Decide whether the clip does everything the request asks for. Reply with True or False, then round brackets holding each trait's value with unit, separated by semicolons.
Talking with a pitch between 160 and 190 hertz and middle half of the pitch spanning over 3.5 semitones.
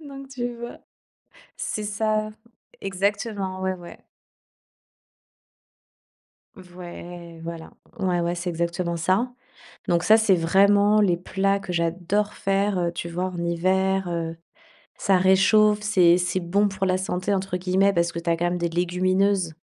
False (185 Hz; 2.6 semitones)